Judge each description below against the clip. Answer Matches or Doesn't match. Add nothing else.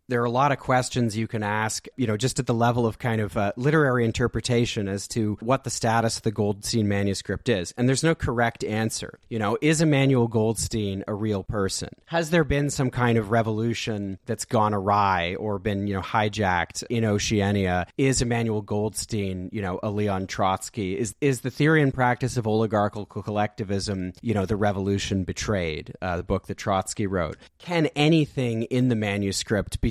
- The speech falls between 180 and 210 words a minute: Matches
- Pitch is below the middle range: Matches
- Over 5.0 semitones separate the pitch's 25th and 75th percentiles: Doesn't match